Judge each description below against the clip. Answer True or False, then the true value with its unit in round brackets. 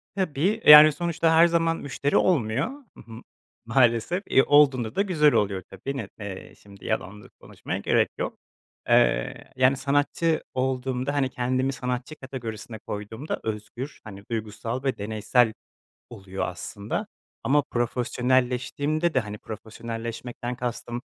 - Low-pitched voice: True (125 Hz)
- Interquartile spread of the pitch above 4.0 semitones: True (4.6 semitones)